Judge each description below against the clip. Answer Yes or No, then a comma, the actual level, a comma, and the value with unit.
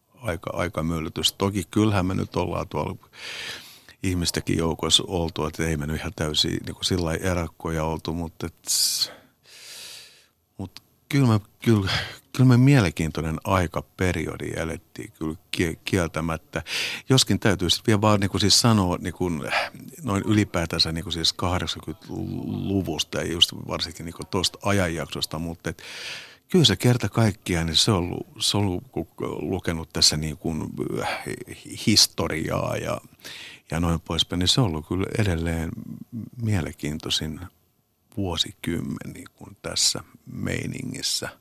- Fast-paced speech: No, average, 130 wpm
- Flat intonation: No, average, 4.2 semitones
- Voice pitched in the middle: No, very low, 90 Hz